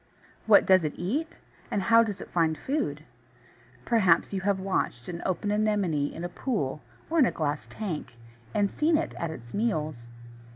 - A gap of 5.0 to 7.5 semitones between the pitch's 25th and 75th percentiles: Yes, wide, 5.6 semitones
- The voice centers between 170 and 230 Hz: Yes, high, 190 Hz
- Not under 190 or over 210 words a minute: No, average, 175 wpm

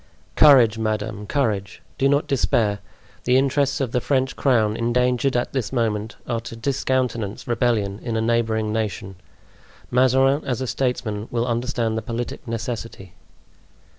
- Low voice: Yes, low, 120 Hz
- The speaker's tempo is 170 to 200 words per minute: No, average, 140 wpm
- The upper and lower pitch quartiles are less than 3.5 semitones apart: Yes, average, 2.9 semitones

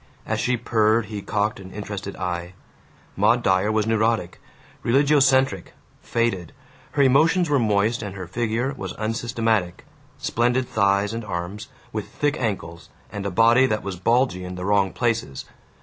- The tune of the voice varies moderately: Yes, average, 3.5 semitones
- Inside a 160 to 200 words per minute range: No, average, 150 wpm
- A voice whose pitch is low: Yes, low, 110 Hz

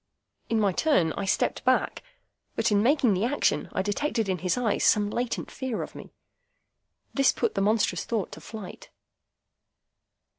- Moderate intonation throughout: Yes, average, 3.8 semitones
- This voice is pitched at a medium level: No, high, 215 Hz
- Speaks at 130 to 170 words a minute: Yes, average, 160 wpm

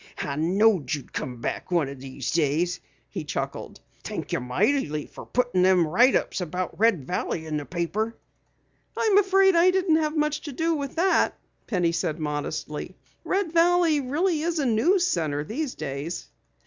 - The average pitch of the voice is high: Yes, high, 210 Hz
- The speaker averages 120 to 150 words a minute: No, average, 170 wpm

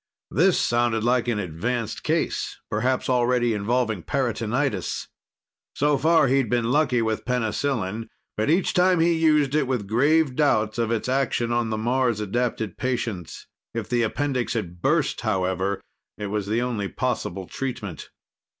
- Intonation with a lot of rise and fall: No, average, 3.8 semitones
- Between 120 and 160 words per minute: Yes, average, 150 wpm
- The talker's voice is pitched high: No, low, 120 Hz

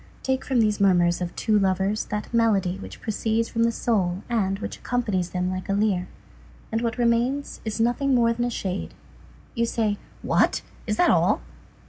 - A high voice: Yes, high, 215 Hz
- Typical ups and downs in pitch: Yes, average, 3.4 semitones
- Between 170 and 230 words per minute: Yes, average, 180 wpm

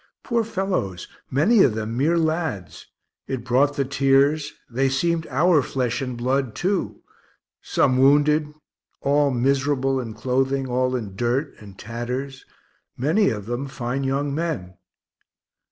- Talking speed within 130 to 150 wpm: Yes, slow, 135 wpm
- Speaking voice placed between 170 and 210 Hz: No, low, 135 Hz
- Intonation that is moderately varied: Yes, average, 3.1 semitones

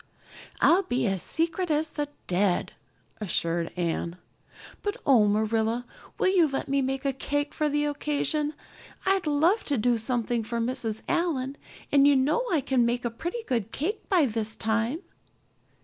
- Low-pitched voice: No, very high, 270 Hz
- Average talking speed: Yes, average, 165 wpm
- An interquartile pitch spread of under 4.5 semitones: No, average, 5.2 semitones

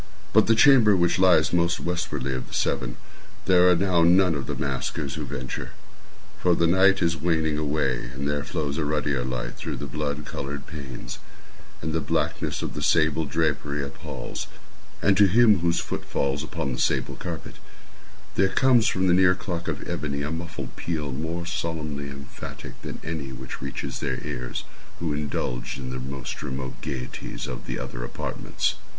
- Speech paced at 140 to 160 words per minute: No, average, 180 wpm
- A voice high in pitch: No, very low, 75 Hz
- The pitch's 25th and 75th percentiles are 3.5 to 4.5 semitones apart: Yes, average, 4.1 semitones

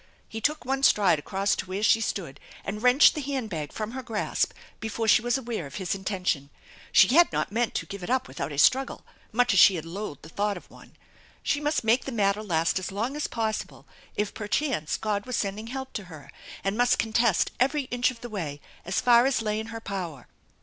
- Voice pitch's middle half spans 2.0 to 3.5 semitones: No, average, 4.4 semitones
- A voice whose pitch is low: No, high, 215 Hz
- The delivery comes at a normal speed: No, fast, 220 wpm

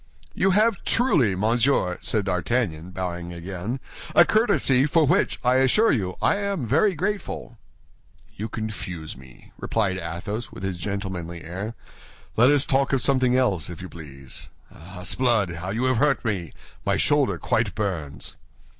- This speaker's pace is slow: No, average, 155 wpm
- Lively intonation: Yes, wide, 6.7 semitones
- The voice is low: Yes, low, 105 Hz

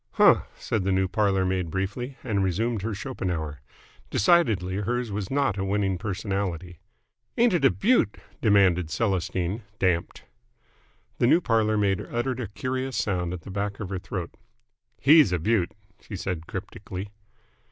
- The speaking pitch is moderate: No, low, 100 Hz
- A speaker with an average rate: Yes, average, 150 wpm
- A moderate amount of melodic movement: Yes, average, 3.9 semitones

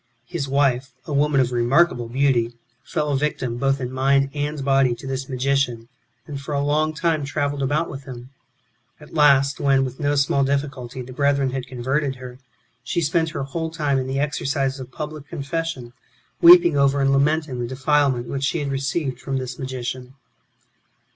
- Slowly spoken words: No, average, 180 wpm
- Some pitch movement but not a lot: No, narrow, 2.0 semitones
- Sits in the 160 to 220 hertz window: No, medium, 140 Hz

